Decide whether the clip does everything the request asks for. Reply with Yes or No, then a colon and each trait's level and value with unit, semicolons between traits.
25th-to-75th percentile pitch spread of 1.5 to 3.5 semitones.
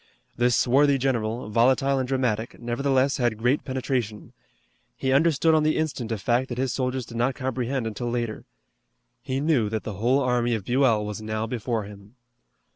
Yes: average, 2.9 semitones